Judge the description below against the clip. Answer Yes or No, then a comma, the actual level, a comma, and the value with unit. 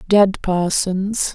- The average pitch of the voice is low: No, high, 190 Hz